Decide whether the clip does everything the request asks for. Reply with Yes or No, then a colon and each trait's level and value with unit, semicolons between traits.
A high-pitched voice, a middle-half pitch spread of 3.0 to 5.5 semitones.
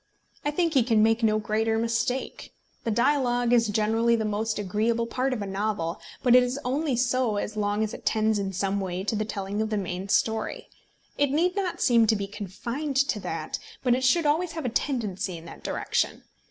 Yes: high, 225 Hz; average, 3.5 semitones